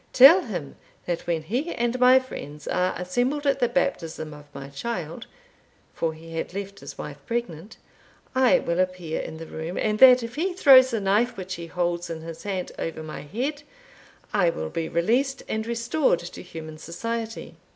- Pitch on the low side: No, high, 190 Hz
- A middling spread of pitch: No, wide, 6.8 semitones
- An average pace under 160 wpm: No, average, 180 wpm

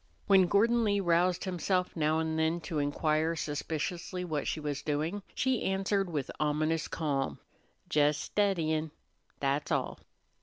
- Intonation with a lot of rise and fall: No, average, 3.5 semitones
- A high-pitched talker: No, medium, 160 Hz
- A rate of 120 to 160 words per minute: Yes, average, 140 wpm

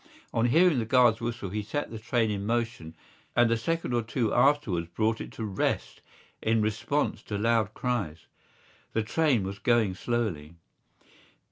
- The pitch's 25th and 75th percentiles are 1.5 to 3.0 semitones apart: Yes, average, 2.7 semitones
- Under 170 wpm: Yes, average, 160 wpm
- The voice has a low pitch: Yes, low, 115 Hz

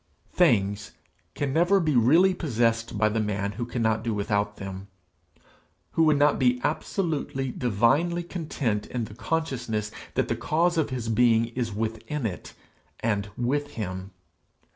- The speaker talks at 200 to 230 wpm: No, average, 145 wpm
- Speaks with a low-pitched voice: Yes, low, 120 Hz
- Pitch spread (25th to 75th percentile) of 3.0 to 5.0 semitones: No, wide, 5.6 semitones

